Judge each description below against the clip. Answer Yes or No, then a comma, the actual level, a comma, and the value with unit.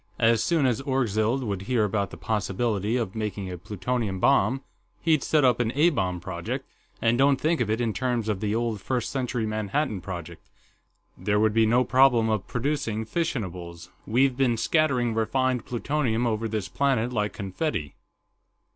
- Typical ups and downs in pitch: Yes, average, 3.8 semitones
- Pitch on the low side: Yes, low, 115 Hz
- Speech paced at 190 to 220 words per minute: No, average, 170 wpm